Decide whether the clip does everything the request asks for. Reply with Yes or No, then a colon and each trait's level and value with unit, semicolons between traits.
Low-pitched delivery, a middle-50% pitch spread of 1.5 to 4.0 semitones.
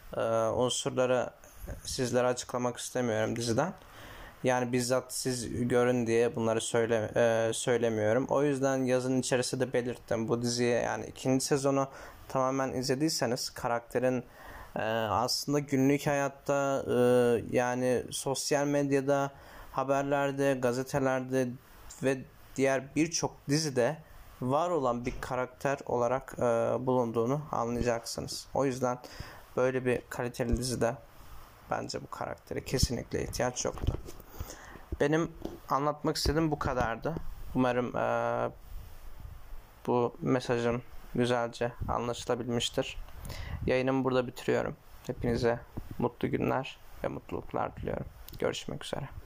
Yes: low, 125 Hz; narrow, 2.4 semitones